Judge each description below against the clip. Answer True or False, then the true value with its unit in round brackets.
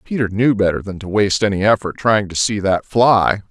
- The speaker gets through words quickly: True (225 wpm)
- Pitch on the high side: False (105 Hz)